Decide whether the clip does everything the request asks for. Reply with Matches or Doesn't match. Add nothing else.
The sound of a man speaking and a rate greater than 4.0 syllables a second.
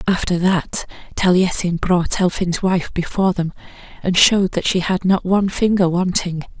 Doesn't match